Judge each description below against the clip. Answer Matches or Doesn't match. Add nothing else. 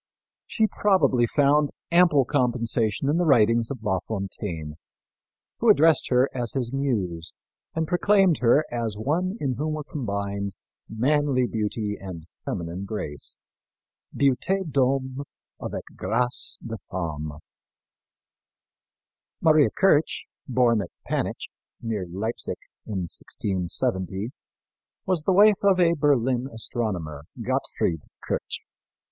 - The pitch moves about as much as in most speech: Doesn't match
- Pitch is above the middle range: Doesn't match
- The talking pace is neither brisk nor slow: Doesn't match